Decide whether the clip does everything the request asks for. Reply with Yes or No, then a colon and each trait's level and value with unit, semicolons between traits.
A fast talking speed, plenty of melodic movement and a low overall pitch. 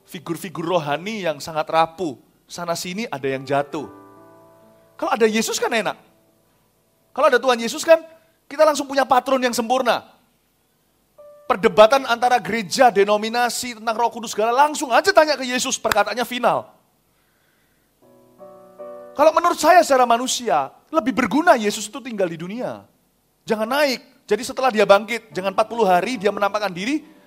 No: fast, 145 wpm; wide, 5.8 semitones; high, 235 Hz